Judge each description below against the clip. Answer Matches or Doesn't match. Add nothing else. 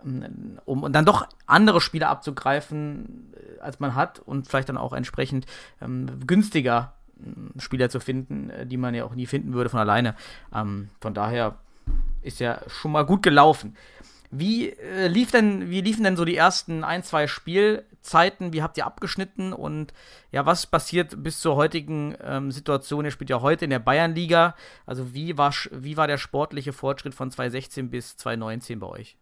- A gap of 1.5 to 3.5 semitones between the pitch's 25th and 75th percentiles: Doesn't match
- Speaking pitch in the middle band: Matches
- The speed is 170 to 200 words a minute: Matches